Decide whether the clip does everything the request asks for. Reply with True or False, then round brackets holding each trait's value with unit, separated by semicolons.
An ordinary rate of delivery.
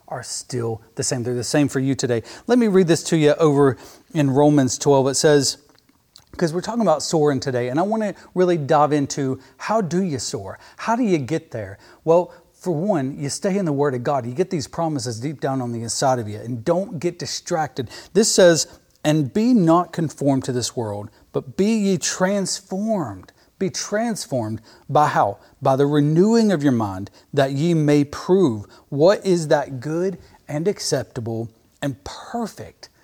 True (190 wpm)